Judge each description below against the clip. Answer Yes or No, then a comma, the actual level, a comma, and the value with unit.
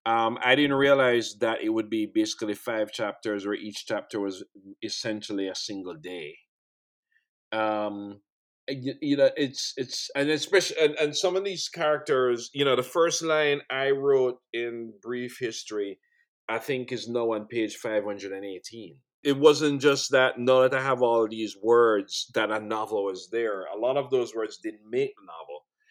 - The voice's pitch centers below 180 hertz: Yes, low, 135 Hz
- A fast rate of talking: No, average, 185 wpm